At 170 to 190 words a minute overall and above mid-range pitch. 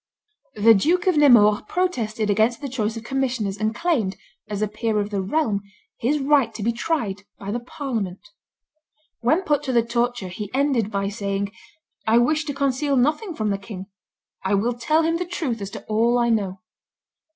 Yes: average, 185 wpm; high, 230 Hz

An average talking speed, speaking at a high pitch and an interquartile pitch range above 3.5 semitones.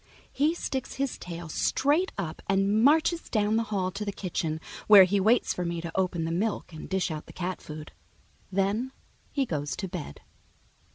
Yes: average, 185 wpm; high, 195 Hz; average, 4.8 semitones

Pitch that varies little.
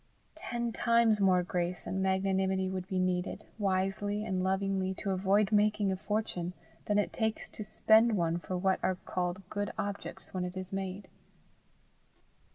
Yes: narrow, 1.9 semitones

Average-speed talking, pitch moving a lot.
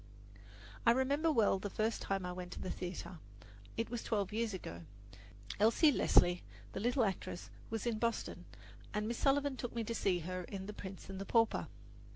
No: average, 190 wpm; average, 3.7 semitones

